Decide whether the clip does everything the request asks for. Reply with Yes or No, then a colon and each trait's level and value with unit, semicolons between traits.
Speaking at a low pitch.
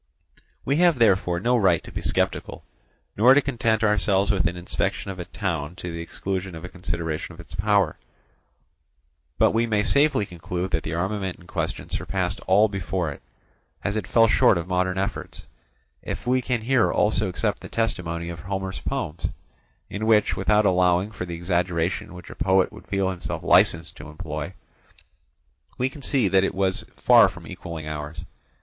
Yes: very low, 95 Hz